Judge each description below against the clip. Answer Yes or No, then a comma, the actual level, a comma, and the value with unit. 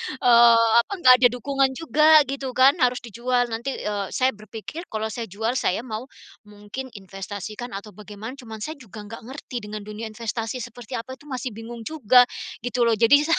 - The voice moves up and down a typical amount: Yes, average, 3.2 semitones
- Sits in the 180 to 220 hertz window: No, high, 235 Hz